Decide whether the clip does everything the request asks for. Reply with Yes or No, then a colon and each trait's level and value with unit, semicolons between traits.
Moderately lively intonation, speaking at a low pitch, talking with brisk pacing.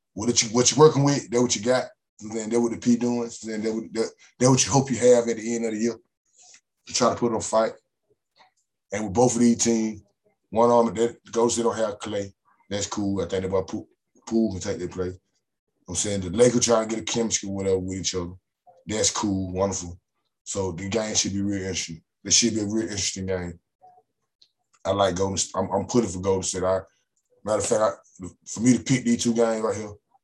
Yes: average, 3.3 semitones; low, 110 Hz; fast, 245 wpm